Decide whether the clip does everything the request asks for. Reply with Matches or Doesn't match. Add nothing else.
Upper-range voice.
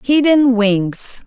Matches